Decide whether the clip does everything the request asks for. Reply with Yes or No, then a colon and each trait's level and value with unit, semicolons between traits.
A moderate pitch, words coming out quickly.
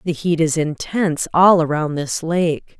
No: medium, 160 Hz; average, 170 wpm